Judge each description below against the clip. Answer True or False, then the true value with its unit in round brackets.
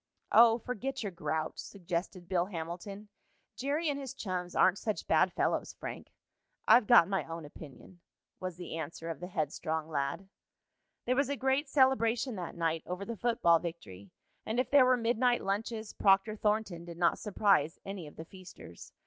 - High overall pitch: True (195 Hz)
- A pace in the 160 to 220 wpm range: True (170 wpm)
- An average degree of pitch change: False (5.7 semitones)